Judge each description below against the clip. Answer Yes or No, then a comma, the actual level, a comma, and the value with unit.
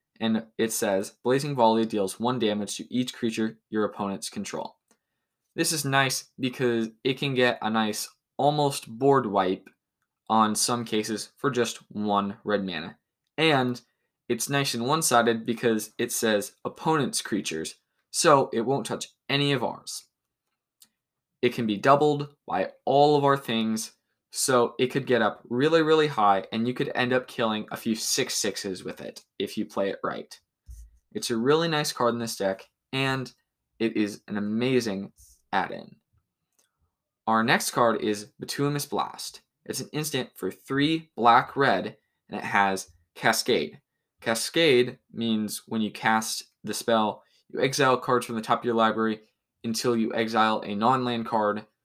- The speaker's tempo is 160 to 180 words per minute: Yes, average, 165 wpm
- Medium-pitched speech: No, low, 115 Hz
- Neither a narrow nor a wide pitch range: Yes, average, 3.4 semitones